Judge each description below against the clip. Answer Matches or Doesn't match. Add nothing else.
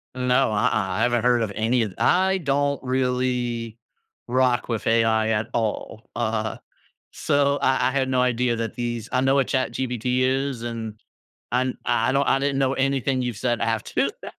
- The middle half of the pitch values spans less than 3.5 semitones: Matches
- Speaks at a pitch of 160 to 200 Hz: Doesn't match